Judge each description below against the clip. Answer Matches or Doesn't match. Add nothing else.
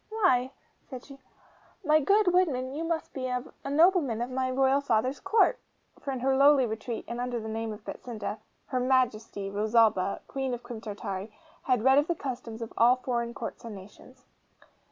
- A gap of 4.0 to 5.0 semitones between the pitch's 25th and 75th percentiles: Doesn't match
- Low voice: Doesn't match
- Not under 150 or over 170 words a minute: Doesn't match